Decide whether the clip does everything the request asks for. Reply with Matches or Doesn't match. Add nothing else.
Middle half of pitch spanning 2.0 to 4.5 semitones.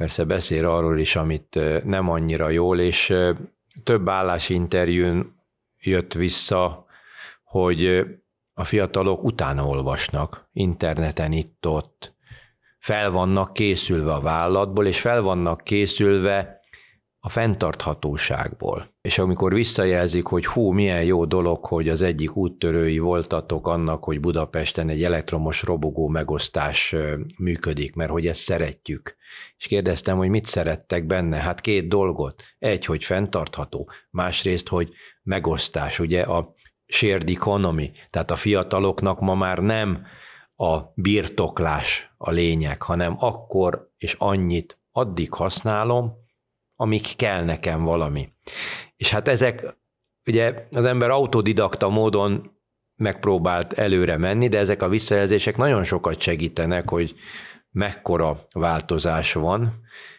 Matches